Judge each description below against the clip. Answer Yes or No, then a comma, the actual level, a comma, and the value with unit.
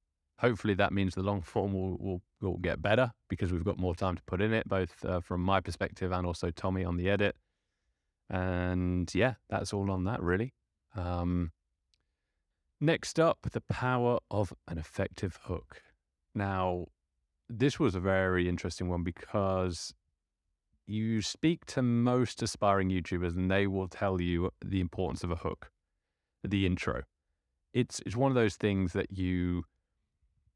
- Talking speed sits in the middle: Yes, average, 160 wpm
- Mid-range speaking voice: No, very low, 95 Hz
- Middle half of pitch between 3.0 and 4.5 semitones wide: No, narrow, 2.6 semitones